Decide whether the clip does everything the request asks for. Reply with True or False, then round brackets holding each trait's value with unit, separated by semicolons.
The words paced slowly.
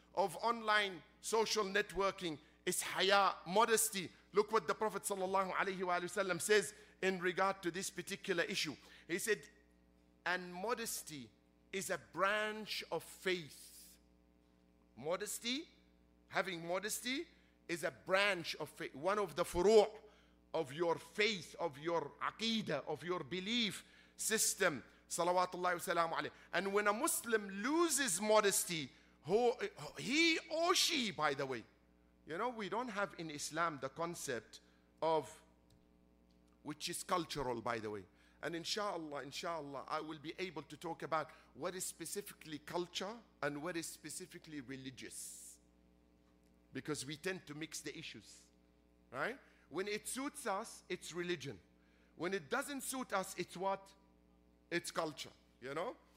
True (130 wpm)